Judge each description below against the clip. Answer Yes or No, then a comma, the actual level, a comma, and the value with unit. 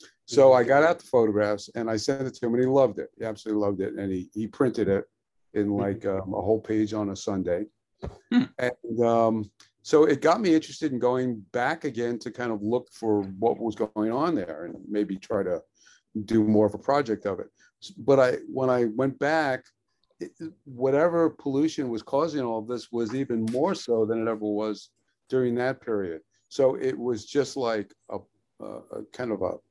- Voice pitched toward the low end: Yes, low, 115 Hz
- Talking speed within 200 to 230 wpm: Yes, fast, 205 wpm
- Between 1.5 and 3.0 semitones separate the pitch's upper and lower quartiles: No, average, 3.8 semitones